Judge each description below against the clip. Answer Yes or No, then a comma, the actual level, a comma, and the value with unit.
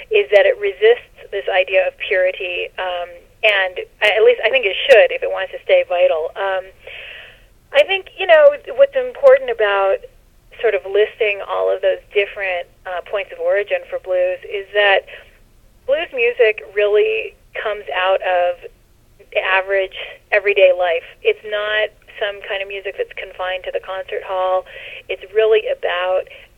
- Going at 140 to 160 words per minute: Yes, average, 155 wpm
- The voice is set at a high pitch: Yes, high, 215 Hz